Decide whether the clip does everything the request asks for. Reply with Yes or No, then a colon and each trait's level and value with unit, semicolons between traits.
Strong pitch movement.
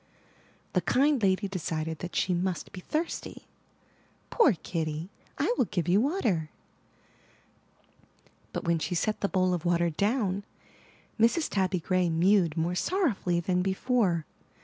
No: average, 3.7 semitones